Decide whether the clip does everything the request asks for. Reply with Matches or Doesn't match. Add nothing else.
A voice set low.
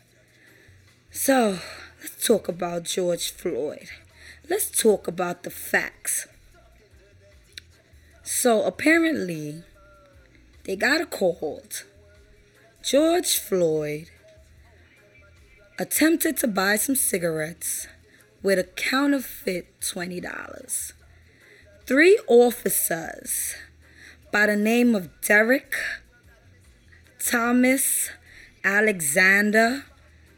Doesn't match